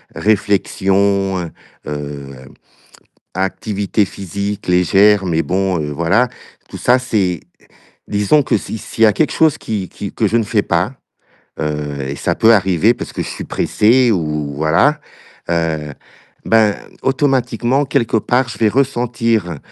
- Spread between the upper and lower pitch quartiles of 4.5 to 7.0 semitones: Yes, average, 5.1 semitones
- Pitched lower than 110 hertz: Yes, low, 100 Hz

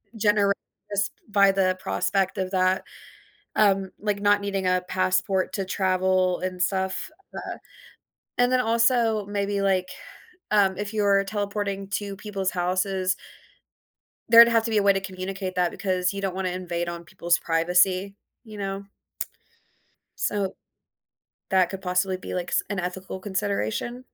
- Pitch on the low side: No, high, 195 Hz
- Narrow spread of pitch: Yes, narrow, 1.7 semitones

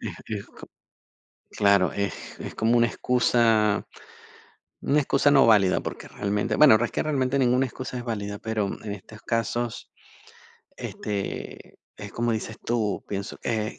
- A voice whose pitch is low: Yes, low, 110 Hz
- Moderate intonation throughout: Yes, average, 3.1 semitones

